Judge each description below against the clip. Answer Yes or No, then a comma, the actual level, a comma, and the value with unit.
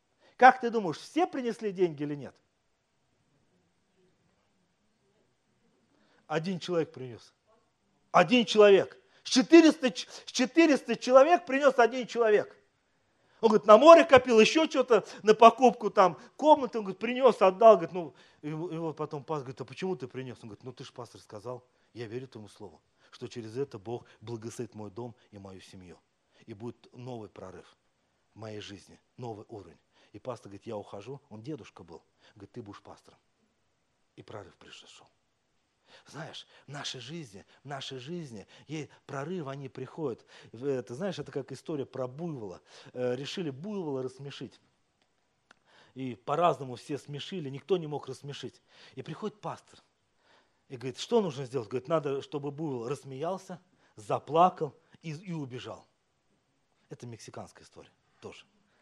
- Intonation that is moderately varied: No, wide, 7.6 semitones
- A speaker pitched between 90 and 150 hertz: Yes, medium, 140 Hz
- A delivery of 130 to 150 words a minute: Yes, average, 140 wpm